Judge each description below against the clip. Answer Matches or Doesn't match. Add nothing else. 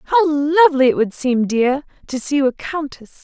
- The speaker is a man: Doesn't match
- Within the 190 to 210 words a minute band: Matches